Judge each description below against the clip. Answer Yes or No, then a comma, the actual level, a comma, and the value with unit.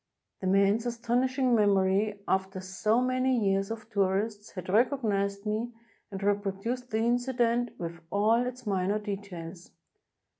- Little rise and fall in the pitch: No, average, 3.5 semitones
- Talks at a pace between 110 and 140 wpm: Yes, slow, 135 wpm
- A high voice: Yes, high, 210 Hz